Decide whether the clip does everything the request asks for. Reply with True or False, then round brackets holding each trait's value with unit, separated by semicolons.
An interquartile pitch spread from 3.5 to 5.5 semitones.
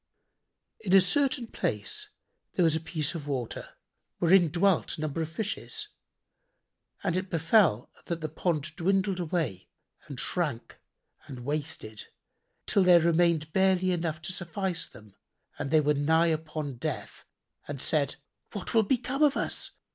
True (3.9 semitones)